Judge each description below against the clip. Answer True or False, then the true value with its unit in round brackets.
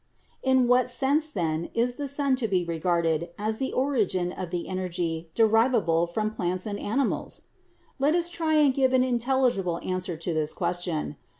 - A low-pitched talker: False (210 Hz)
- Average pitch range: False (7.2 semitones)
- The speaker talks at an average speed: True (170 wpm)